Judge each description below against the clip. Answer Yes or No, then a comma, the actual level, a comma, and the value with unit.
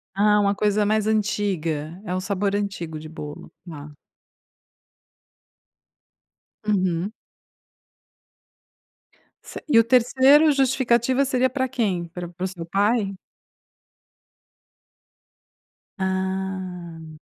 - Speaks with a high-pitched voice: Yes, high, 200 Hz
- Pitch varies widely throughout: No, average, 4.5 semitones